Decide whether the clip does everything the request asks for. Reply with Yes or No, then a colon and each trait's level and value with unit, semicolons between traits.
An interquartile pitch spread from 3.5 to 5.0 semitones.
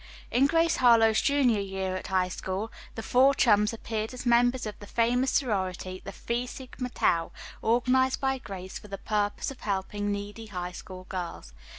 Yes: average, 4.5 semitones